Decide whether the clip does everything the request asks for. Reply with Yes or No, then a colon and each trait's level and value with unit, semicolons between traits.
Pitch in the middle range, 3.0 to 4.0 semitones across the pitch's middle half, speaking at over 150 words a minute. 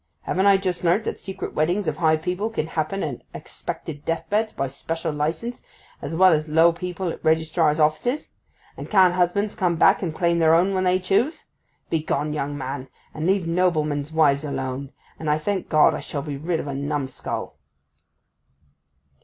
Yes: medium, 160 Hz; average, 3.5 semitones; average, 180 wpm